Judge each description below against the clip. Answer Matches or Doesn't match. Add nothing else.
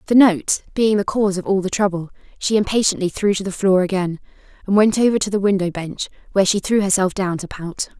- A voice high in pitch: Matches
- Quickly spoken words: Matches